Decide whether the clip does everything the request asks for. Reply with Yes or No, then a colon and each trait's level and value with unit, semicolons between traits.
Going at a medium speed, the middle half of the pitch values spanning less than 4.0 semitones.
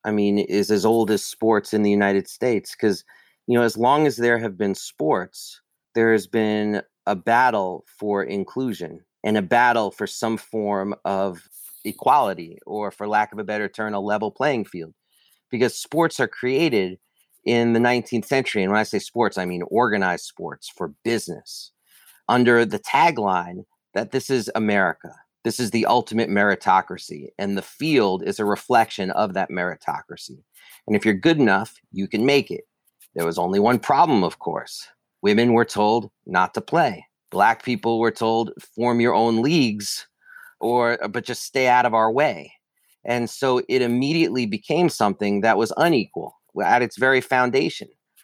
Yes: average, 170 wpm; average, 3.0 semitones